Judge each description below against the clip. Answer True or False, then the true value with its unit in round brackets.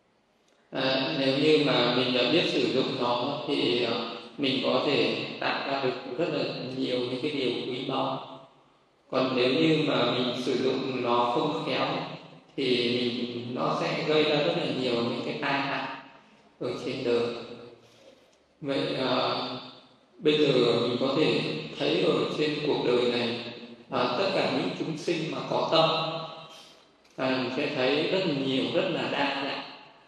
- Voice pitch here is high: False (130 Hz)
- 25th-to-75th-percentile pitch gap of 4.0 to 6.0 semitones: False (3.3 semitones)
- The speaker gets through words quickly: False (165 wpm)